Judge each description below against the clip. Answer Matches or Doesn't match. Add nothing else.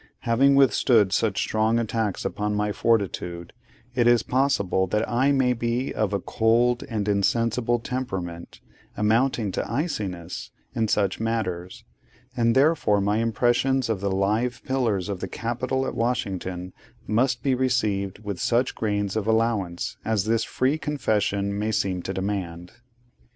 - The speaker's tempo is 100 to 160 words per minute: Matches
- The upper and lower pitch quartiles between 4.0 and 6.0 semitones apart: Doesn't match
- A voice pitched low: Matches